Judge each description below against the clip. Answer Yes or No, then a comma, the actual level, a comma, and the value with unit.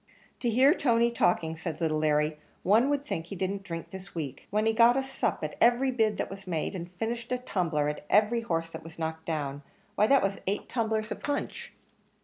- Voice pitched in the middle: No, high, 195 Hz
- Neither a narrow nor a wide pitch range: No, wide, 6.2 semitones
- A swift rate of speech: Yes, fast, 210 wpm